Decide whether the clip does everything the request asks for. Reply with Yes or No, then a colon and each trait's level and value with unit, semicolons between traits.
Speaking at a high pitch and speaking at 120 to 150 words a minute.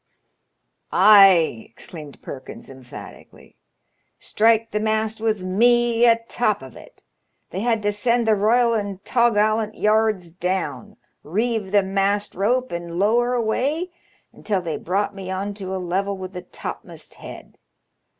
Yes: high, 205 Hz; slow, 135 wpm